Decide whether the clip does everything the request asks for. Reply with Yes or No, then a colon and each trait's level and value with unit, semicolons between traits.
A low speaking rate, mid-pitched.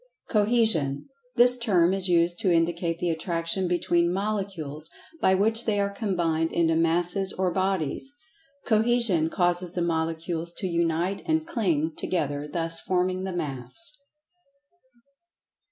Yes: slow, 125 wpm; medium, 175 Hz